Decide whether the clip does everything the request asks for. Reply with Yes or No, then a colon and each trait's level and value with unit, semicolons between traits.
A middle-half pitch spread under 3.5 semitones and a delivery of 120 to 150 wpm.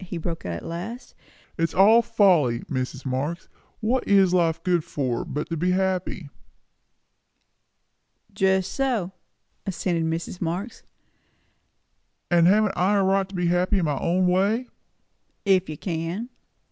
Yes: average, 2.9 semitones; average, 145 wpm